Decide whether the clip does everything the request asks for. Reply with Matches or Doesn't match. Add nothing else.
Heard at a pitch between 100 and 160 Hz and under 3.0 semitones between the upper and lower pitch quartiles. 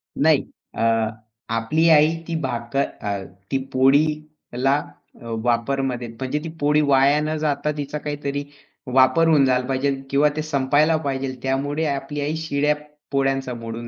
Matches